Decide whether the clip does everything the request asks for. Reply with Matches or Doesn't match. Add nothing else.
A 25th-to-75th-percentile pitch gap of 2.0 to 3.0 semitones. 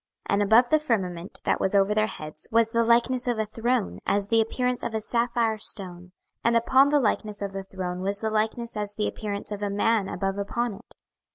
Matches